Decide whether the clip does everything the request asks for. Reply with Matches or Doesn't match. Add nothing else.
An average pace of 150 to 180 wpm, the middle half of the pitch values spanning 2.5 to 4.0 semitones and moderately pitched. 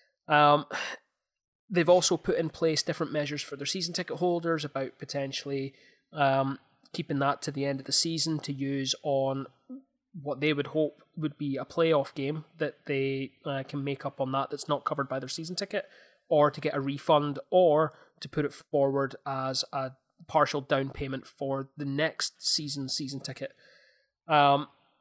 Matches